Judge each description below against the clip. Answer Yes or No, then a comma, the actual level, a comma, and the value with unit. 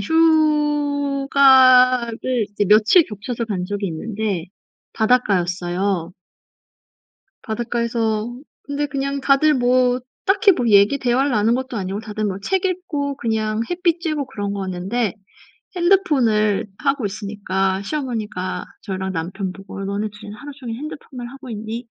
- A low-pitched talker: No, high, 235 Hz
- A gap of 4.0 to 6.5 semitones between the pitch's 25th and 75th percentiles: Yes, average, 5.3 semitones